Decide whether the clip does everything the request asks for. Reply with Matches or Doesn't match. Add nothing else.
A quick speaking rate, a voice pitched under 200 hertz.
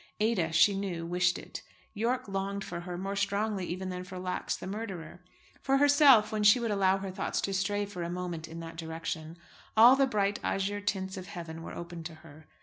Matches